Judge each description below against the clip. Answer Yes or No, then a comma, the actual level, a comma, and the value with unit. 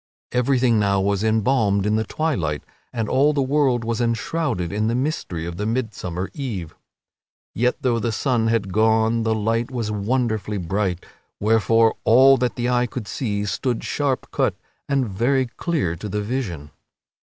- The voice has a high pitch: No, low, 115 Hz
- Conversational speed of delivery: Yes, average, 165 wpm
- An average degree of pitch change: Yes, average, 3.7 semitones